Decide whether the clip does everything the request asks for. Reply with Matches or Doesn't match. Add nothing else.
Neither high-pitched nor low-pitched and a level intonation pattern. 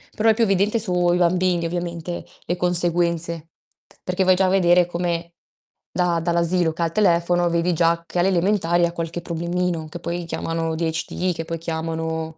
Matches